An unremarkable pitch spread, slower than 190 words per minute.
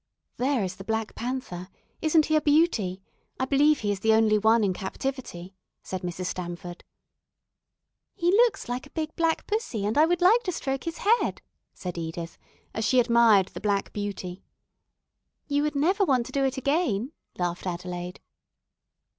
No: wide, 8.1 semitones; average, 170 wpm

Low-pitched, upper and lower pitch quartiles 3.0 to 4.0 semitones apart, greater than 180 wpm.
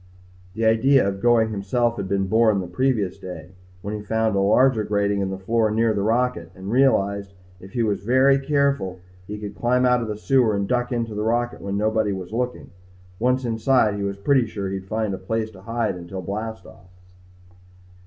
Yes: low, 110 Hz; average, 3.4 semitones; fast, 205 wpm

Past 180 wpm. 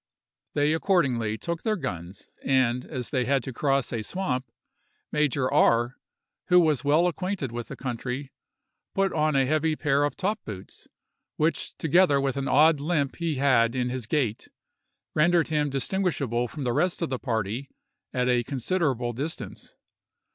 No: average, 160 wpm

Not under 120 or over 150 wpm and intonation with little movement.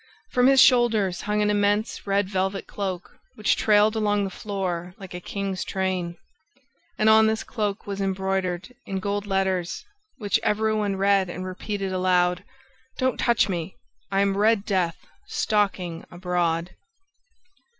Yes: average, 145 wpm; narrow, 2.1 semitones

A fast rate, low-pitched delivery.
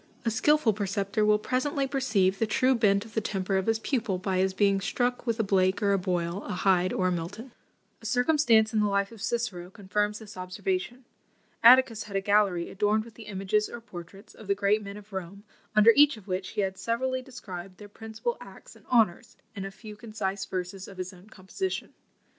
No: fast, 210 wpm; high, 210 Hz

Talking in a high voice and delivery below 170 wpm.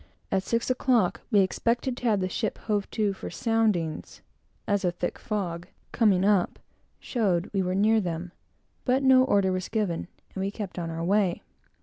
No: high, 200 Hz; average, 180 wpm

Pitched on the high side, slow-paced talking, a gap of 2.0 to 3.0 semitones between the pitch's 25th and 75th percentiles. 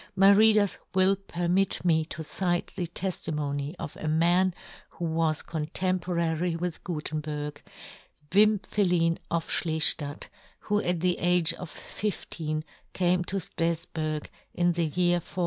No: medium, 170 Hz; slow, 130 wpm; narrow, 2.4 semitones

